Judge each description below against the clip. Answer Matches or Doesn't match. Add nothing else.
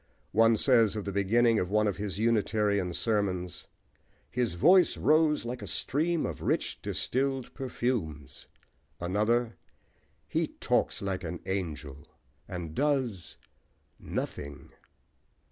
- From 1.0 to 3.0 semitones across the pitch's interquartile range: Doesn't match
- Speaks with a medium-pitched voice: Doesn't match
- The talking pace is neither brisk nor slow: Doesn't match